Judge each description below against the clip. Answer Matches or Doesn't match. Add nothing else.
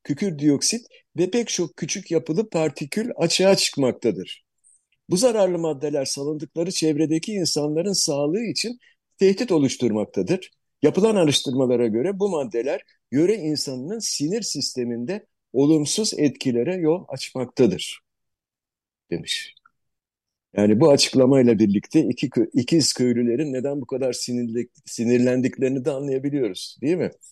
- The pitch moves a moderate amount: Doesn't match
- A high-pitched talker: Doesn't match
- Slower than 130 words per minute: Matches